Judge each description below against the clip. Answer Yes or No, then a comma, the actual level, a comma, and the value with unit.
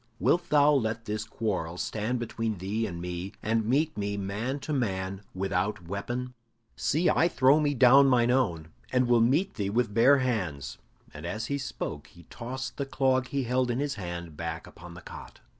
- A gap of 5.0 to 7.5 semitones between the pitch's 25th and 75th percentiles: Yes, wide, 5.4 semitones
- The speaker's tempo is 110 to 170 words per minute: No, average, 190 wpm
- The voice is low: Yes, low, 115 Hz